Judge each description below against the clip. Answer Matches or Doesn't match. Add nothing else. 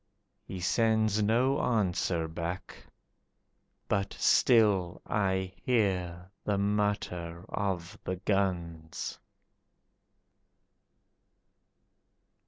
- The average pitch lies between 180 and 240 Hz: Doesn't match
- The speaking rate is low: Matches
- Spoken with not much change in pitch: Doesn't match